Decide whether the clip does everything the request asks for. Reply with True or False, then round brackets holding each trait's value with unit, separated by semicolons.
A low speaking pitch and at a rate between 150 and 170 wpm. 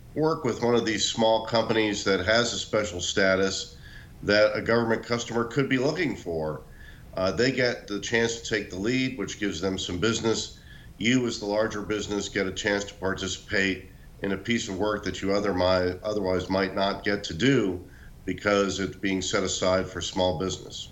False (100 Hz; 185 wpm)